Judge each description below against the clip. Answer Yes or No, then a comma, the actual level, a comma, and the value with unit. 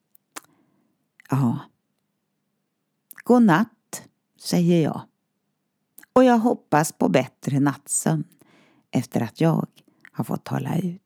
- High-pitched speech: Yes, high, 200 Hz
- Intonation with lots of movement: Yes, wide, 6.1 semitones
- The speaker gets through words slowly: Yes, slow, 100 wpm